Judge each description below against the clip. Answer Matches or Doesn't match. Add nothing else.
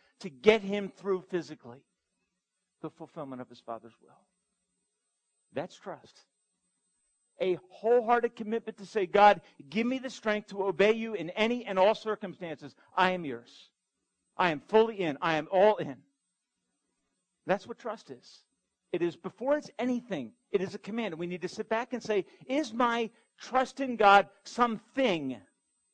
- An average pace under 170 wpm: Matches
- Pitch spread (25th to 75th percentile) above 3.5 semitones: Matches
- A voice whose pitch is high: Matches